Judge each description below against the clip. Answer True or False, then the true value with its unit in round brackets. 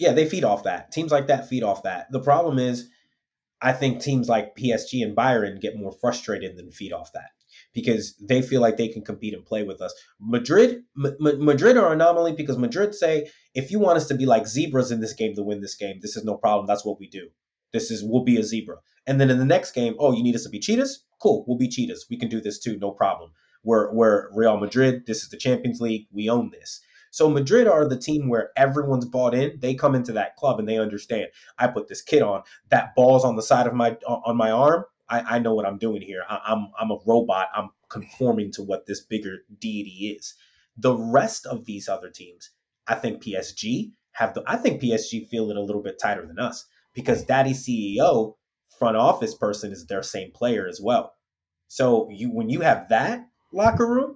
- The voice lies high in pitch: False (125 Hz)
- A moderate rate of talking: False (230 wpm)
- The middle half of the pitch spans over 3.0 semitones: True (4.4 semitones)